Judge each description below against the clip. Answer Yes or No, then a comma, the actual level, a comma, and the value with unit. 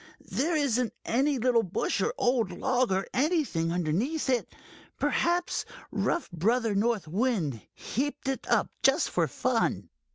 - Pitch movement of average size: No, wide, 6.0 semitones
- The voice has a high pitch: Yes, high, 245 Hz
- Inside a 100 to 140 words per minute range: Yes, slow, 135 wpm